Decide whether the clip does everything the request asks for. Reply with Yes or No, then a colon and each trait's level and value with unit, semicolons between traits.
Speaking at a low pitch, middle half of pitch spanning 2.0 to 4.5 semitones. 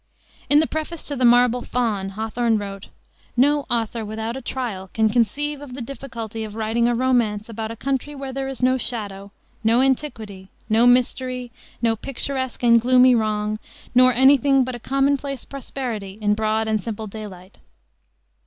No: high, 235 Hz; average, 3.2 semitones